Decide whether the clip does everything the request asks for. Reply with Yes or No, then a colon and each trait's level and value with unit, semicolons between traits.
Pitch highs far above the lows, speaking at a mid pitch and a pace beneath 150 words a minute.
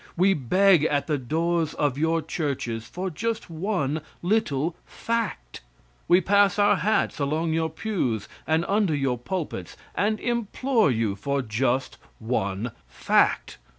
Yes: wide, 6.9 semitones; medium, 160 Hz; slow, 135 wpm